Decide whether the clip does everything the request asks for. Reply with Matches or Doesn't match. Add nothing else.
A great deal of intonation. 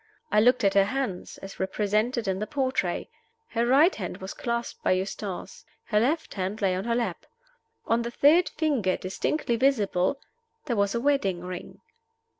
Doesn't match